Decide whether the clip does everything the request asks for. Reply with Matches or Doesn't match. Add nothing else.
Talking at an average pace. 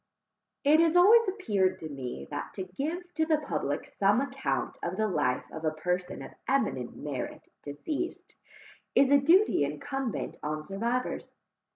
Matches